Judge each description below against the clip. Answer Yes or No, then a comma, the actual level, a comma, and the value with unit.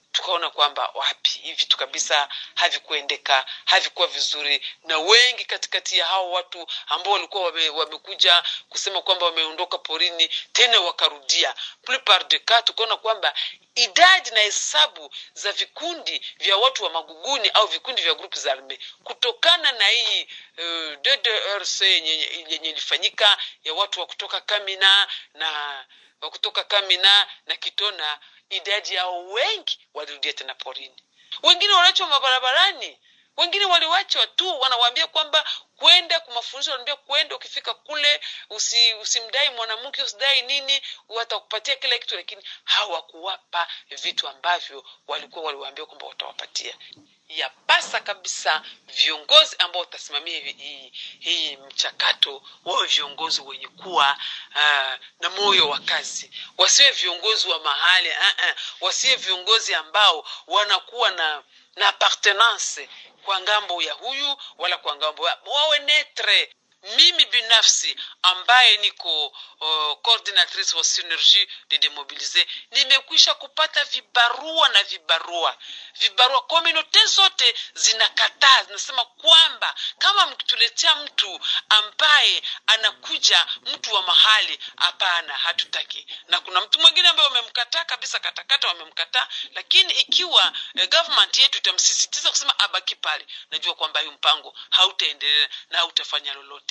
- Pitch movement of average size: No, wide, 8.8 semitones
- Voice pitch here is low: No, high, 215 Hz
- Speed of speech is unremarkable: No, slow, 120 wpm